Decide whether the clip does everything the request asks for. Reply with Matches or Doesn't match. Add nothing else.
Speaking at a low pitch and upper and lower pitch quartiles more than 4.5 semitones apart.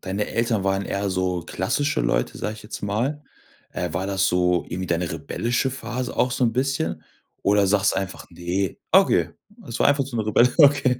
Matches